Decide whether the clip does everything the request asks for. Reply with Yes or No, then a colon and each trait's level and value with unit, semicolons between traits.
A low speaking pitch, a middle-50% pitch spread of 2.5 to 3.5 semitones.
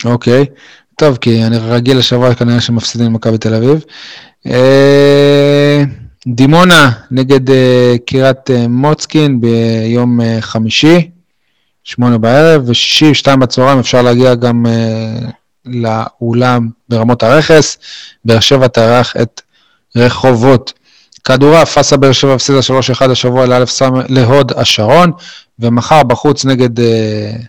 Yes: low, 125 Hz; average, 2.8 semitones